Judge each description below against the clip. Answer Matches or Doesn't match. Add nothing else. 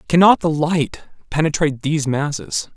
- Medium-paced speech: Doesn't match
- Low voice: Doesn't match